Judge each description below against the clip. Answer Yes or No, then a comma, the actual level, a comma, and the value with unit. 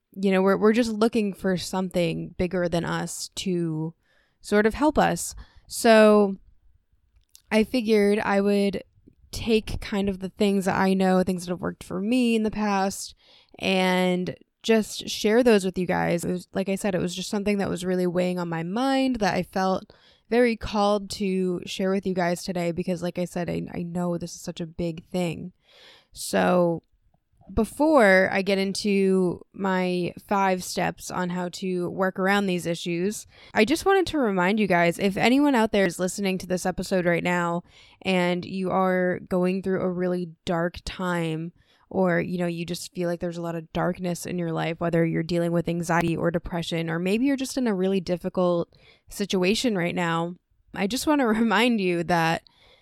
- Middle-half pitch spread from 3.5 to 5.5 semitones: No, narrow, 2.5 semitones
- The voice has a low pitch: No, medium, 185 Hz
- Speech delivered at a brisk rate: No, average, 190 wpm